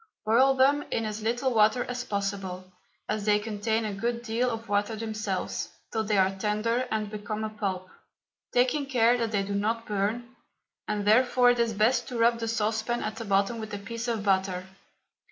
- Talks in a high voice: Yes, high, 220 Hz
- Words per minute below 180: No, average, 190 wpm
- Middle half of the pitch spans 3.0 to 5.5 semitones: No, narrow, 2.4 semitones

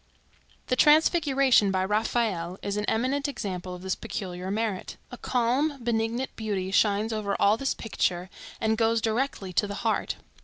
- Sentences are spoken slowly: No, average, 155 wpm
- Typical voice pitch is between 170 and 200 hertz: No, high, 220 Hz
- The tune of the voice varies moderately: Yes, average, 4.2 semitones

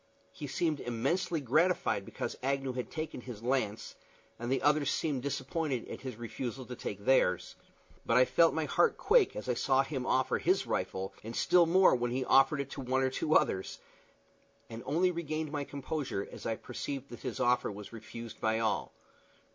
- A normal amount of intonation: Yes, average, 4.2 semitones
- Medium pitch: No, low, 130 Hz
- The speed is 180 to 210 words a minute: Yes, average, 185 wpm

